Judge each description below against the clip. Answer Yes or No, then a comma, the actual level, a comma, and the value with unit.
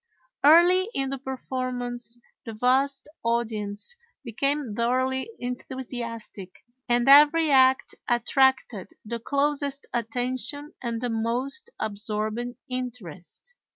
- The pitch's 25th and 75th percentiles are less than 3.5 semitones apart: Yes, average, 2.8 semitones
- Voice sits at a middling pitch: No, very high, 250 Hz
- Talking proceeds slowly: Yes, slow, 95 wpm